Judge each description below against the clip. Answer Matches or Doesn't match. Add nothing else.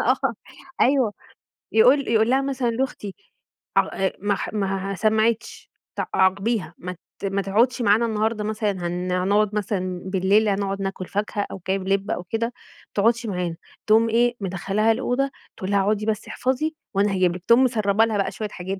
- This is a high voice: Matches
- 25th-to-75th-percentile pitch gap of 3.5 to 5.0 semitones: Doesn't match